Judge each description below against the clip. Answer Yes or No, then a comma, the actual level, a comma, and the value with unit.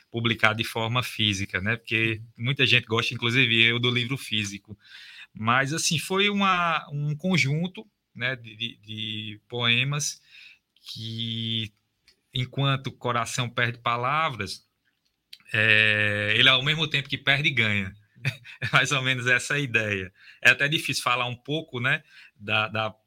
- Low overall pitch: Yes, low, 120 Hz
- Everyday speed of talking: Yes, average, 140 wpm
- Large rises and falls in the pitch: No, average, 3.9 semitones